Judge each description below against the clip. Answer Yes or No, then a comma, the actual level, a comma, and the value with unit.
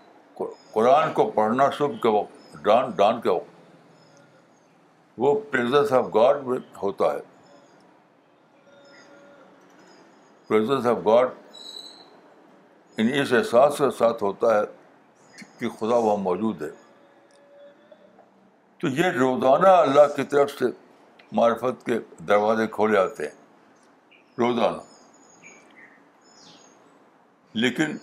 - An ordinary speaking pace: No, slow, 100 wpm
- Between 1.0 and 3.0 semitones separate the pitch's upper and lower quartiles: No, average, 4.6 semitones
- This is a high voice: No, low, 130 Hz